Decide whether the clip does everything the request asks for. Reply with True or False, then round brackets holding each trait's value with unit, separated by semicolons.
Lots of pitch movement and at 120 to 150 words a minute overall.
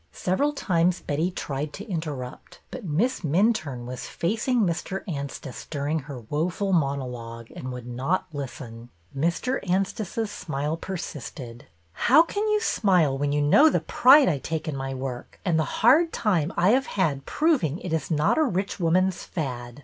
False (6.2 semitones; 165 wpm)